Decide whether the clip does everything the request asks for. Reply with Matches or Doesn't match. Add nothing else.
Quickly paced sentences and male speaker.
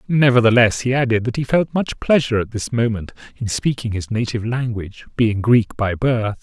Doesn't match